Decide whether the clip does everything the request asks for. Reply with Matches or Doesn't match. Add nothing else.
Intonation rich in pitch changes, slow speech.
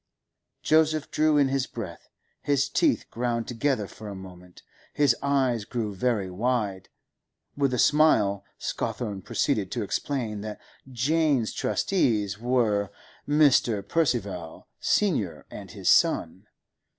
Matches